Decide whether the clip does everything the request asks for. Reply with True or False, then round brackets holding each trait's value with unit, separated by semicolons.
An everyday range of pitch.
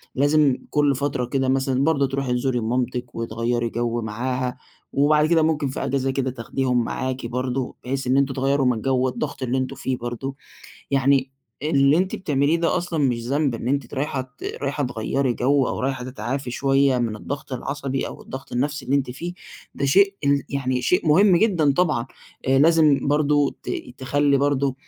False (2.2 semitones)